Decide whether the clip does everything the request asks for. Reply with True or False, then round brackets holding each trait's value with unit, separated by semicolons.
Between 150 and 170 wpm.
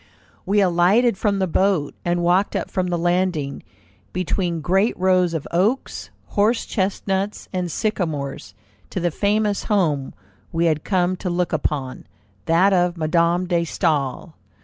False (140 wpm)